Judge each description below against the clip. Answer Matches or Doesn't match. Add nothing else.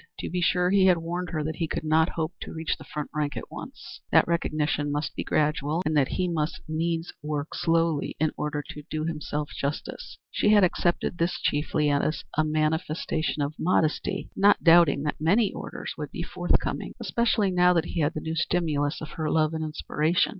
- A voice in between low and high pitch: Matches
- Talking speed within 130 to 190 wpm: Doesn't match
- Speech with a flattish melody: Matches